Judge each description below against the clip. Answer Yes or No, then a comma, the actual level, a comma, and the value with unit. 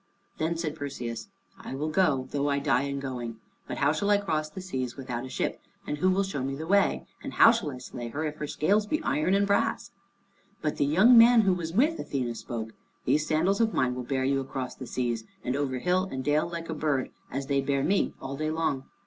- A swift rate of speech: Yes, fast, 235 wpm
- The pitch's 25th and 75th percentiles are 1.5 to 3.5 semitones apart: No, wide, 5.4 semitones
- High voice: No, medium, 145 Hz